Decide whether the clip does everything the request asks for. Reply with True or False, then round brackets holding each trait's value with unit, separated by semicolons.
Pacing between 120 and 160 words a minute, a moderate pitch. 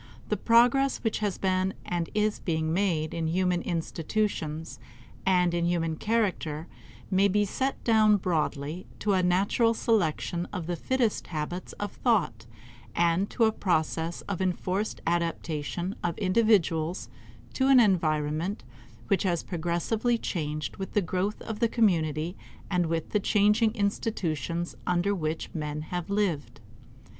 True (140 wpm; 180 Hz)